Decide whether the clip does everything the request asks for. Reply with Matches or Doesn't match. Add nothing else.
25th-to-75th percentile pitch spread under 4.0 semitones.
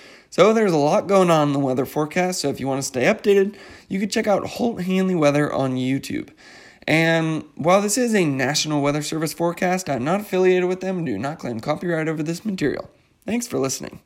Doesn't match